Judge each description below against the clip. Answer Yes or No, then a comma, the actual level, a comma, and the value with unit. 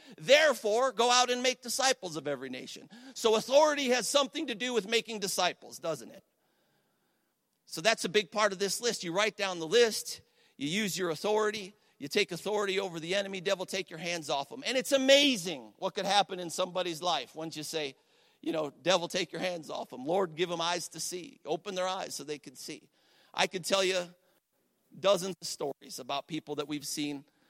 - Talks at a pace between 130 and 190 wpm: No, fast, 205 wpm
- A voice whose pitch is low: No, high, 190 Hz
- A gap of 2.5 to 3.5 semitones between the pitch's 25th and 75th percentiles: No, average, 5.0 semitones